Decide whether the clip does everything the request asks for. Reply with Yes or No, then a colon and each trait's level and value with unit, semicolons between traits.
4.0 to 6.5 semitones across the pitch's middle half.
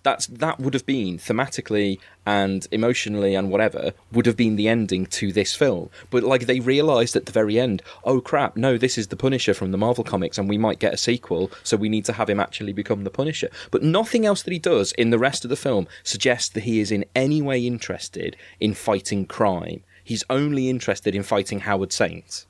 Yes: average, 4.4 semitones